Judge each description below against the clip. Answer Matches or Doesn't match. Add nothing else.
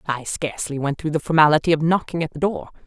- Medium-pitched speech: Matches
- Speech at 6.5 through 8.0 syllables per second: Matches